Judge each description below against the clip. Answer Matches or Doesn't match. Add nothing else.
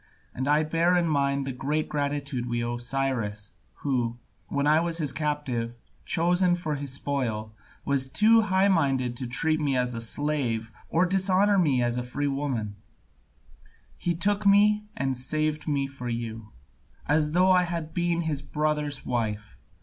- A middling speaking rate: Matches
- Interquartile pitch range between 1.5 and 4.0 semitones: Doesn't match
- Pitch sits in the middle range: Matches